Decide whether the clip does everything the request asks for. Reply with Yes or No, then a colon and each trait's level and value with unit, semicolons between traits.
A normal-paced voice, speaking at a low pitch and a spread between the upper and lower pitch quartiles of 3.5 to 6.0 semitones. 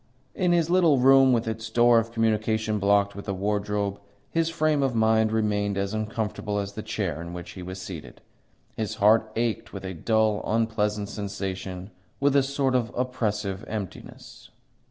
No: average, 170 wpm; low, 110 Hz; average, 2.8 semitones